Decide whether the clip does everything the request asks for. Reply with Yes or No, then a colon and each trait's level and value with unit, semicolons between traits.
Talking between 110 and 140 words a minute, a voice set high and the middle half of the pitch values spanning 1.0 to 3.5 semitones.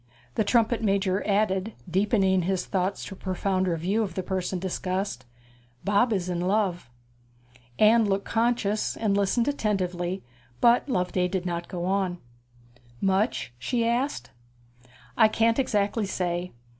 Yes: slow, 135 wpm; high, 195 Hz; average, 3.0 semitones